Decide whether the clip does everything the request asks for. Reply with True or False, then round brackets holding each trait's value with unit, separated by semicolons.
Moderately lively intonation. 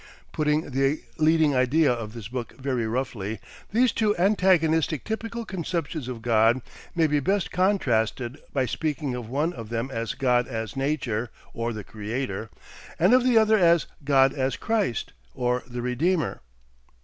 False (5.8 semitones)